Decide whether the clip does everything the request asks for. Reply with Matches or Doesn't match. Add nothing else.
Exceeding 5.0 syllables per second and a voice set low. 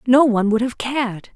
Doesn't match